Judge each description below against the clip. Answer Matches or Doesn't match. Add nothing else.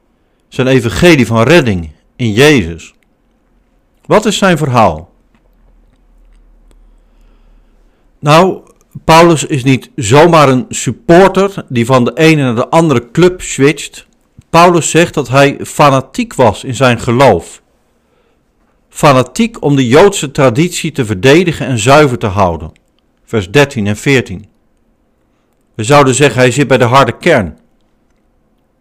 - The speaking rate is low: Matches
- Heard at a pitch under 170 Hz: Matches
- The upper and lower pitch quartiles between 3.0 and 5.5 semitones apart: Matches